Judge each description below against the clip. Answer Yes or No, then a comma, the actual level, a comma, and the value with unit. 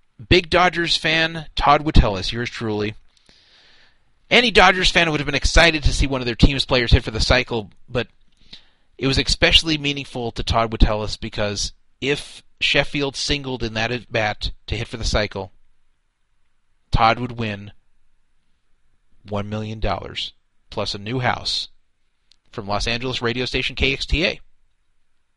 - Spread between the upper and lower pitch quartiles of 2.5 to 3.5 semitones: No, average, 5.0 semitones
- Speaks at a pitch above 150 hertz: No, low, 115 Hz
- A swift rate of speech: No, average, 145 wpm